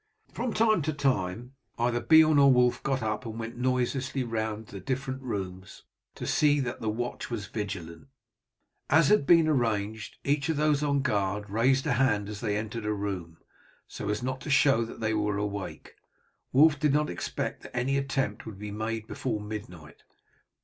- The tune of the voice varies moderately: Yes, average, 4.7 semitones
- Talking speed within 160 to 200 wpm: Yes, average, 180 wpm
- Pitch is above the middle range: No, low, 120 Hz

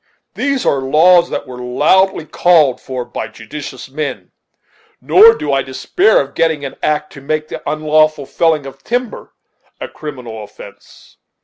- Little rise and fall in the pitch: No, average, 4.2 semitones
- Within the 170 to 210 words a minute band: No, average, 150 wpm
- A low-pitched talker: No, medium, 150 Hz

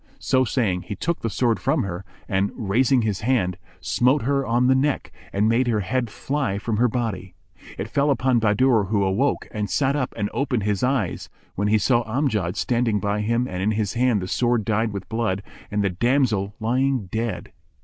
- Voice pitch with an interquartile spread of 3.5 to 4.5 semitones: Yes, average, 3.9 semitones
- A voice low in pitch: Yes, low, 110 Hz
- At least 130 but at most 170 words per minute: No, average, 200 wpm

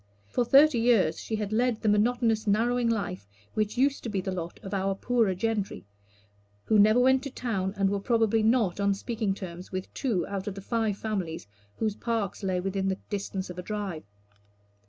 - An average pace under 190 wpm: No, average, 195 wpm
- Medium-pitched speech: No, high, 210 Hz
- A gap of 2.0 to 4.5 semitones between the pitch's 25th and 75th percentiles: Yes, average, 3.1 semitones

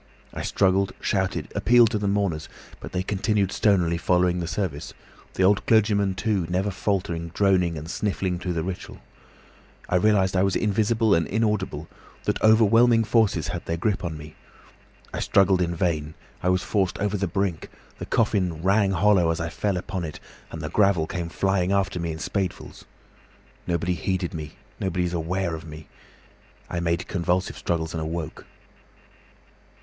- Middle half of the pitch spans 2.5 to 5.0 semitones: Yes, average, 3.0 semitones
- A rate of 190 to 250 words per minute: No, average, 165 wpm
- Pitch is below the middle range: Yes, very low, 95 Hz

